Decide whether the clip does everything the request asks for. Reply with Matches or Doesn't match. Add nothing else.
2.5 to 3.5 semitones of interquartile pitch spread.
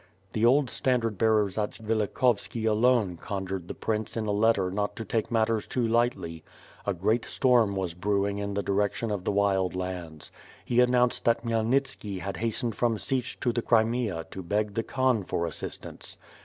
Matches